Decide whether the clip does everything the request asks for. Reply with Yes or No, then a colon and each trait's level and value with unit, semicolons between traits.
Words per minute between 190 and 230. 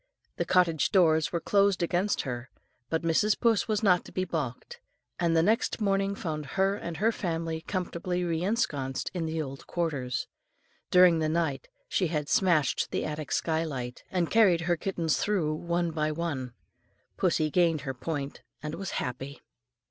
No: average, 165 wpm